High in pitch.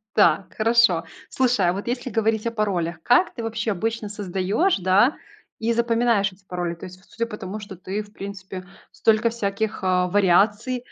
Yes: high, 210 Hz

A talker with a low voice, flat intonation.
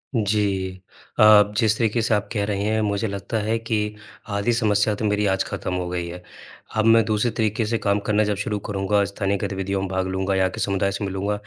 Yes: low, 105 Hz; narrow, 1.8 semitones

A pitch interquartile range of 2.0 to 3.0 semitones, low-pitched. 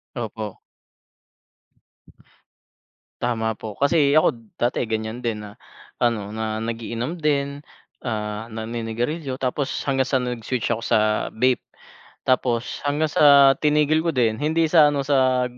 No: average, 4.0 semitones; low, 125 Hz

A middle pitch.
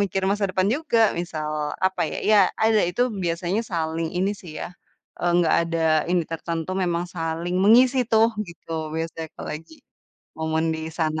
Yes: medium, 175 Hz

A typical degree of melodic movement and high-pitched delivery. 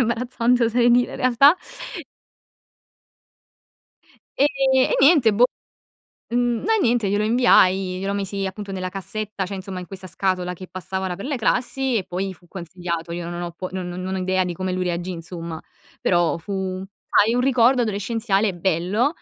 Yes: average, 4.3 semitones; high, 195 Hz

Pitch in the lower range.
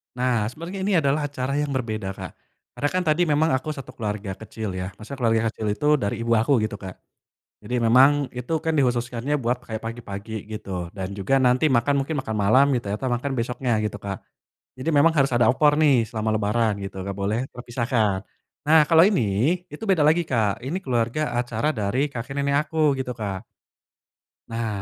Yes: low, 125 Hz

